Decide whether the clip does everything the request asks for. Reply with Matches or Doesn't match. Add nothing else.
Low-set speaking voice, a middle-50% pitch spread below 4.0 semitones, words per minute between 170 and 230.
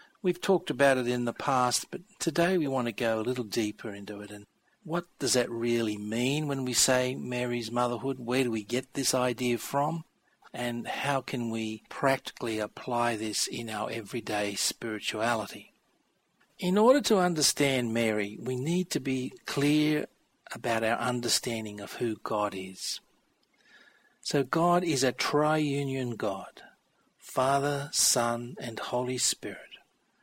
Doesn't match